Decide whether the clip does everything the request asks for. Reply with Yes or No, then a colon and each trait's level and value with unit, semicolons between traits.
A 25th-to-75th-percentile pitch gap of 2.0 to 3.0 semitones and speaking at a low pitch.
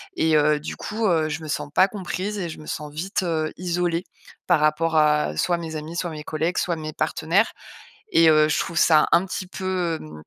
No: narrow, 2.5 semitones; medium, 165 Hz